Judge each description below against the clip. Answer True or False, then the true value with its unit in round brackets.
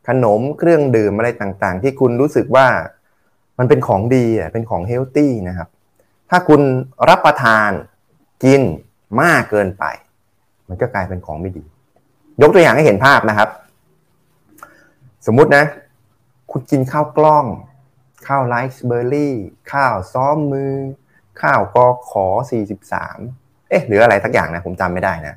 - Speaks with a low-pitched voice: True (125 Hz)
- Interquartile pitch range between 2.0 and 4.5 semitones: False (4.9 semitones)